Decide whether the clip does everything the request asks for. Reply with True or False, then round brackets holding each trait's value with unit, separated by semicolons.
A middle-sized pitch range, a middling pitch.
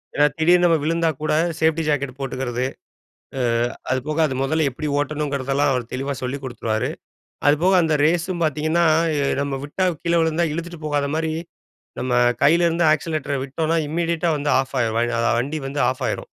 True (3.3 semitones; 150 Hz)